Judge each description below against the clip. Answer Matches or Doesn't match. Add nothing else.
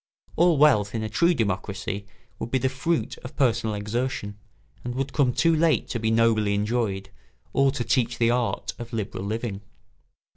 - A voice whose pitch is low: Matches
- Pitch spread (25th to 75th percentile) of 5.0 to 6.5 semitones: Doesn't match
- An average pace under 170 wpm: Doesn't match